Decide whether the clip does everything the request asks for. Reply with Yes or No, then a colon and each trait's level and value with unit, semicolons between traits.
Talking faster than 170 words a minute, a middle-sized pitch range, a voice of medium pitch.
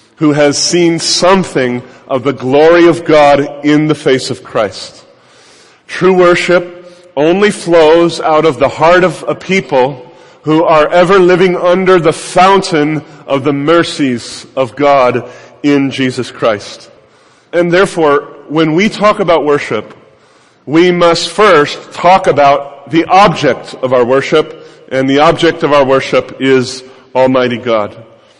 No: average, 140 wpm; average, 4.4 semitones; medium, 150 Hz